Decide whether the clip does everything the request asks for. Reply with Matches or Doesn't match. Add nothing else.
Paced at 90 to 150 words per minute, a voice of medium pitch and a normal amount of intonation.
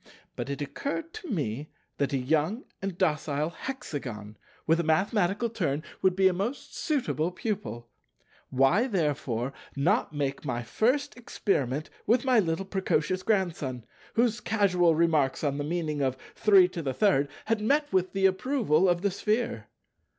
Doesn't match